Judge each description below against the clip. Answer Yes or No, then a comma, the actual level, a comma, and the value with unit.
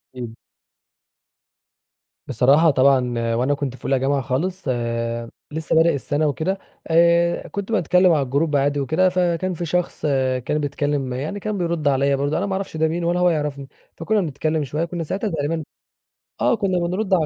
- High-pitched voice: No, medium, 155 Hz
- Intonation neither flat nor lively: Yes, average, 4.1 semitones